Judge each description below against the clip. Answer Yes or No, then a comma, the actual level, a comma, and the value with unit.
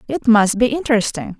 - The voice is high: Yes, high, 235 Hz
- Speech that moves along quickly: No, average, 170 wpm